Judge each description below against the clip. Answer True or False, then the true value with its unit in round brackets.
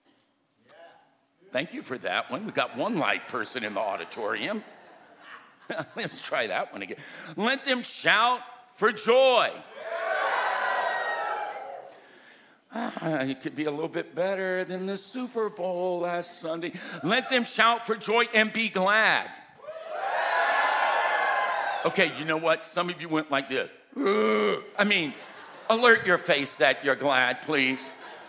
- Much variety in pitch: True (6.8 semitones)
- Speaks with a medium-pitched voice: False (195 Hz)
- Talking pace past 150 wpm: False (135 wpm)